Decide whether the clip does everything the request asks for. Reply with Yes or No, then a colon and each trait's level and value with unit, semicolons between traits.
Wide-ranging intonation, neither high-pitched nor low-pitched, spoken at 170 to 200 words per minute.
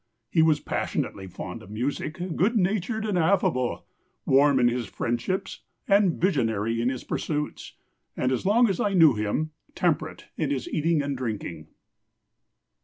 No: wide, 7.8 semitones; medium, 145 Hz; average, 150 wpm